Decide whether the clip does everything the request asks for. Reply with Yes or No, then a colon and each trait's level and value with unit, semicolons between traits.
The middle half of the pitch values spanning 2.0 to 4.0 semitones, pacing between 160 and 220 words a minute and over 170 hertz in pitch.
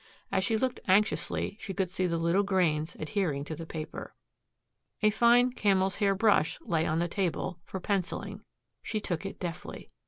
Yes: average, 3.4 semitones; average, 175 wpm; high, 190 Hz